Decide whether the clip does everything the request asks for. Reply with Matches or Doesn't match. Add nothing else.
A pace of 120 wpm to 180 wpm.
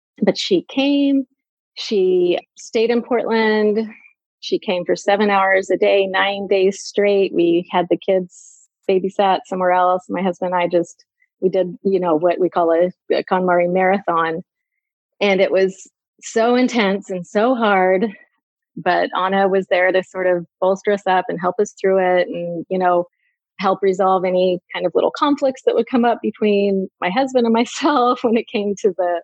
Matches